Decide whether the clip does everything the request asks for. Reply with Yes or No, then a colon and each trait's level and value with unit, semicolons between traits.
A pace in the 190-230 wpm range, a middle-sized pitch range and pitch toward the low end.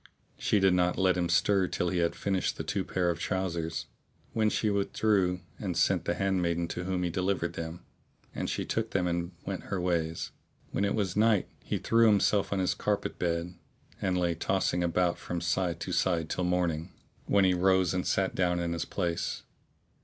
No: average, 200 wpm; narrow, 1.9 semitones; very low, 90 Hz